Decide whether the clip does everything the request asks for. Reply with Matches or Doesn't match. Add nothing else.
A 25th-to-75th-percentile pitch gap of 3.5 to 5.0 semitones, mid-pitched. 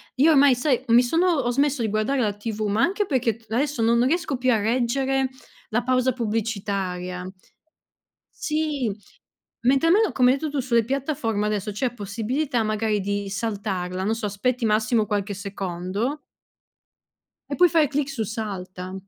Doesn't match